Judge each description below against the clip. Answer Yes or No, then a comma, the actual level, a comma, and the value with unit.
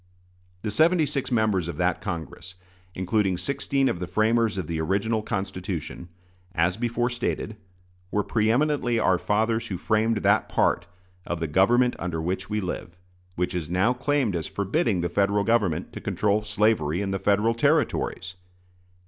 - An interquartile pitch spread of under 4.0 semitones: No, average, 4.3 semitones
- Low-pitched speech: Yes, low, 105 Hz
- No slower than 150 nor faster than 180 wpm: Yes, average, 160 wpm